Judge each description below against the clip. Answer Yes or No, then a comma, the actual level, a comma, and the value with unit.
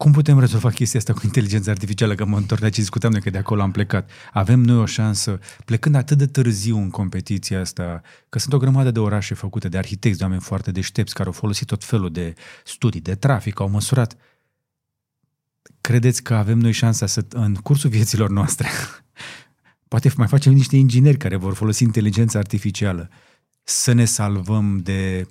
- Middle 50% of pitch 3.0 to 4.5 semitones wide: Yes, average, 3.5 semitones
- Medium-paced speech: No, fast, 185 wpm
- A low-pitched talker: Yes, low, 110 Hz